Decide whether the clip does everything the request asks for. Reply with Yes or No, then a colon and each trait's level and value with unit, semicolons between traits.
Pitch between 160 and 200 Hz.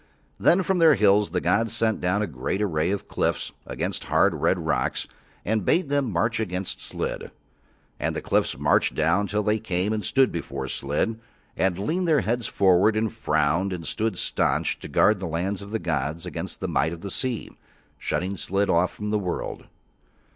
No: low, 100 Hz